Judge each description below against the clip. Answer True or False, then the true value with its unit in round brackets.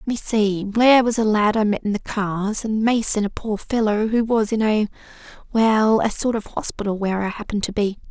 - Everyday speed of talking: False (220 wpm)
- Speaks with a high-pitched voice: True (215 Hz)